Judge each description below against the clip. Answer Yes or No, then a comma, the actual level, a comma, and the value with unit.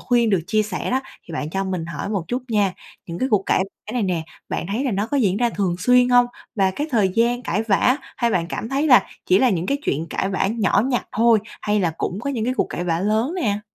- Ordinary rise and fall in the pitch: Yes, average, 4.4 semitones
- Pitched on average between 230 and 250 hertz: No, high, 215 Hz